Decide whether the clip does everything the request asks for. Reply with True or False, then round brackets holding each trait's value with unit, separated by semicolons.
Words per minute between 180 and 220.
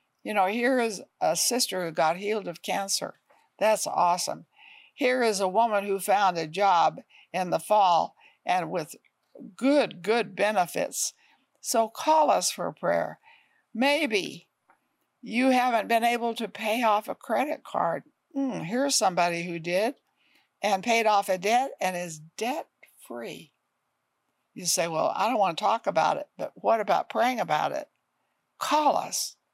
False (160 wpm)